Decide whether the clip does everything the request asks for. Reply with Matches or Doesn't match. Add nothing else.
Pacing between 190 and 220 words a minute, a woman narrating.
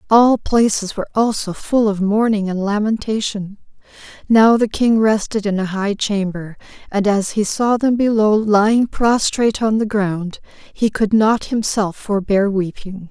Doesn't match